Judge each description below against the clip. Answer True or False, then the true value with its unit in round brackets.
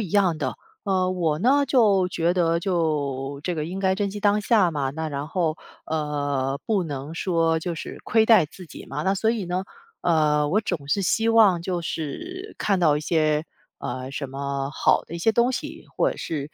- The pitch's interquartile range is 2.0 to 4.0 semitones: False (4.7 semitones)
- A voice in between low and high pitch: True (170 Hz)